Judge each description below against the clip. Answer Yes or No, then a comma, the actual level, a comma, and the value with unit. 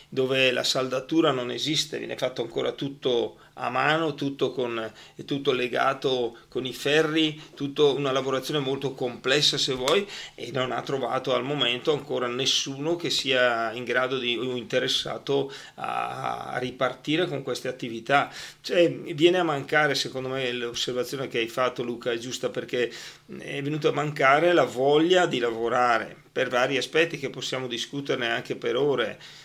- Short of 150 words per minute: No, average, 160 wpm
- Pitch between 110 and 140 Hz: Yes, low, 135 Hz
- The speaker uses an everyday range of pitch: Yes, average, 3.1 semitones